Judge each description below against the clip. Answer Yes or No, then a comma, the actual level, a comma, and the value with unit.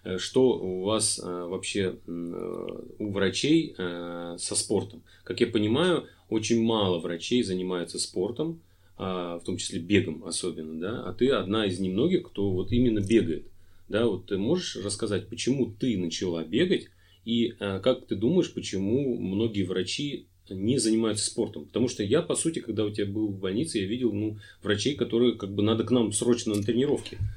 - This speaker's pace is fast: Yes, fast, 170 wpm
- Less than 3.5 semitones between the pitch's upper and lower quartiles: No, average, 4.1 semitones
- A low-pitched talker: Yes, low, 105 Hz